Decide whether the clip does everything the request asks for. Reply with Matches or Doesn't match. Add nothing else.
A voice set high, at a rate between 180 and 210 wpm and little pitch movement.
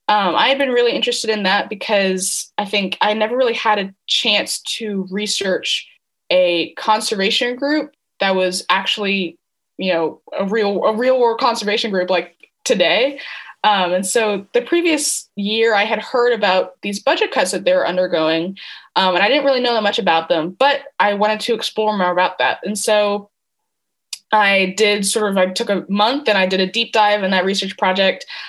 Doesn't match